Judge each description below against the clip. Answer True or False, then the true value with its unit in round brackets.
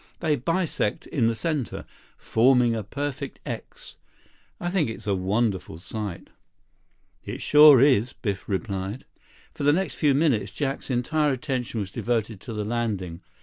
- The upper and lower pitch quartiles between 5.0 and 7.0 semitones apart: True (5.6 semitones)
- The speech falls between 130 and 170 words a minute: True (145 wpm)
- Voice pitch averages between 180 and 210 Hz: False (120 Hz)